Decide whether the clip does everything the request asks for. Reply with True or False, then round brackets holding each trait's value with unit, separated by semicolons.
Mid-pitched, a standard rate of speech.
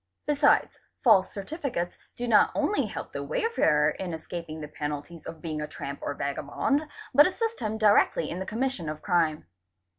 True (175 Hz; 170 wpm)